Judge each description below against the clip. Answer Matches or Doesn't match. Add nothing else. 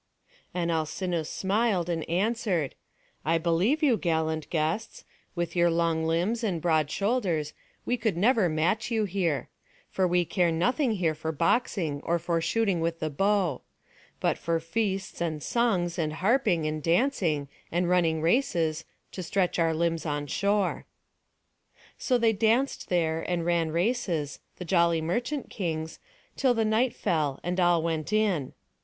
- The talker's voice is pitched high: Doesn't match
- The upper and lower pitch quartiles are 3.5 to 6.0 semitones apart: Matches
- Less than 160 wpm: Matches